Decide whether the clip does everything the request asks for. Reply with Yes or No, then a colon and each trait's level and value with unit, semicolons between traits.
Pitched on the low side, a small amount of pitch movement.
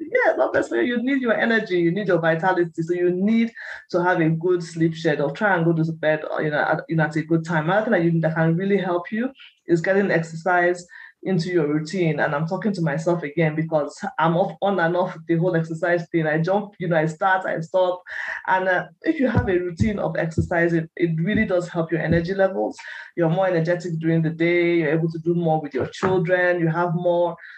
No: medium, 175 Hz; narrow, 2.2 semitones